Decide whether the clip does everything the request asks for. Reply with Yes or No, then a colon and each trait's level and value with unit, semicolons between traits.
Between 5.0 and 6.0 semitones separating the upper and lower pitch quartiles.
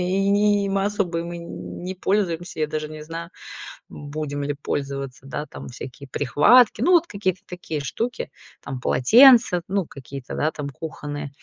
Yes: wide, 5.4 semitones